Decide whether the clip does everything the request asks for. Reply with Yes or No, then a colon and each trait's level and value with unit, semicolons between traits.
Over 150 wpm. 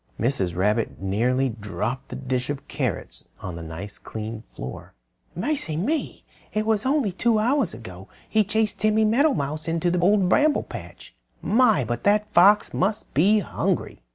Yes: average, 165 wpm